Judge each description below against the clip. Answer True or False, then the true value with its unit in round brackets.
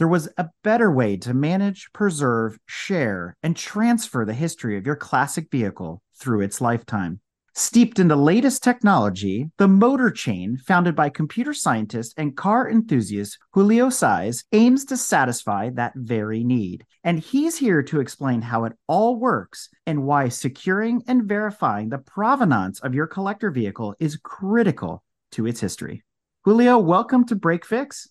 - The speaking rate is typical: True (155 wpm)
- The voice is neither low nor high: True (160 Hz)